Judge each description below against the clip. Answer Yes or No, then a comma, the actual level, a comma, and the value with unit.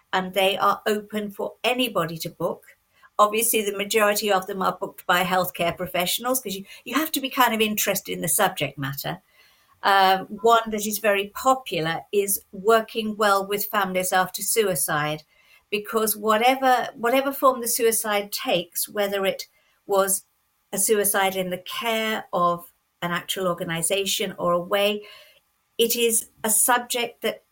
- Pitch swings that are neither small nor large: Yes, average, 3.3 semitones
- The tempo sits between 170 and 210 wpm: No, average, 155 wpm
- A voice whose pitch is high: Yes, high, 205 Hz